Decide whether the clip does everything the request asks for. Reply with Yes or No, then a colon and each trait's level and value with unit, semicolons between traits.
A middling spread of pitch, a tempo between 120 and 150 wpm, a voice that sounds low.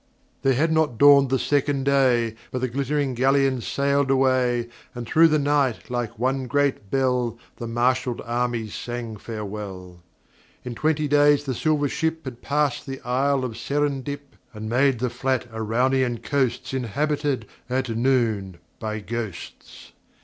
Yes: average, 3.1 semitones; average, 145 wpm; low, 130 Hz